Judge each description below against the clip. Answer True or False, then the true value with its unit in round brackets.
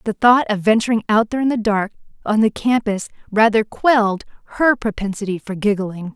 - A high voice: True (215 Hz)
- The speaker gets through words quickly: False (175 wpm)